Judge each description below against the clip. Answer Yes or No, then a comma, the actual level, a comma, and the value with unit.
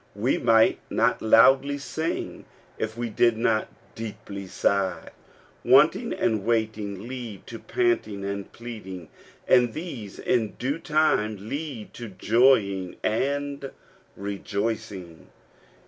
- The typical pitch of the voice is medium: No, low, 110 Hz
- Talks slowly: Yes, slow, 110 wpm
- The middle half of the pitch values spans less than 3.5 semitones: No, average, 4.3 semitones